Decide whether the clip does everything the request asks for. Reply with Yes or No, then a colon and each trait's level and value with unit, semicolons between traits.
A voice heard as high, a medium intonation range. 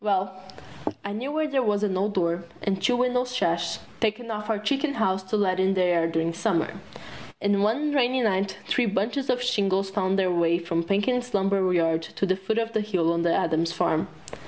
Yes: high, 200 Hz; average, 4.1 semitones